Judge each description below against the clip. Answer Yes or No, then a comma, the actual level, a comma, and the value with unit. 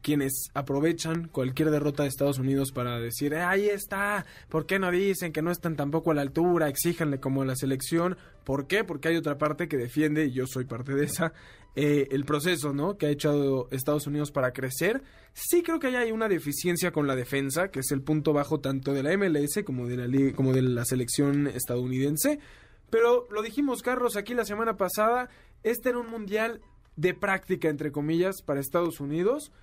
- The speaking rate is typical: No, fast, 205 wpm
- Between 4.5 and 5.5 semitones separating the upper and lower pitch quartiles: Yes, average, 5.2 semitones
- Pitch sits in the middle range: Yes, medium, 150 Hz